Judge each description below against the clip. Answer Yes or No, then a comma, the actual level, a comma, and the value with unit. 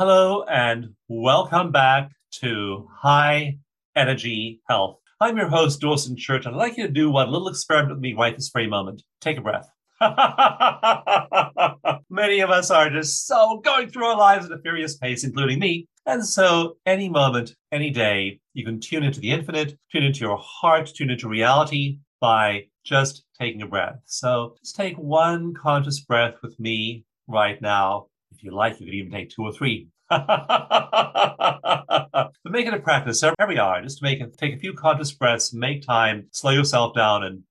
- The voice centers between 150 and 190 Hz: No, medium, 140 Hz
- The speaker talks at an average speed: Yes, average, 180 wpm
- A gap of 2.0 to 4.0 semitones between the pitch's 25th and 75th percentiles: No, wide, 5.6 semitones